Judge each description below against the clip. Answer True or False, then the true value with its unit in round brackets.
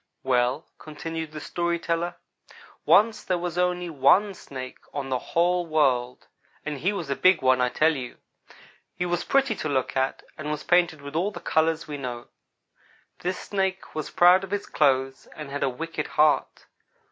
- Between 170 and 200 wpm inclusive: True (180 wpm)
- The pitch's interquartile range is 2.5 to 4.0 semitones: False (4.5 semitones)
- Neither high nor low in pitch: True (155 Hz)